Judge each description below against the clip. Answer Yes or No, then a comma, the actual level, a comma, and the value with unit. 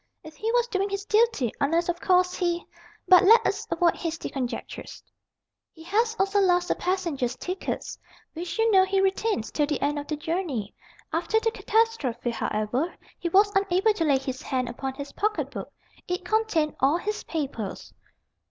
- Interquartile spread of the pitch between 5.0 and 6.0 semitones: Yes, wide, 5.6 semitones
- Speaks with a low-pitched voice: No, very high, 350 Hz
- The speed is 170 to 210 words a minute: Yes, average, 175 wpm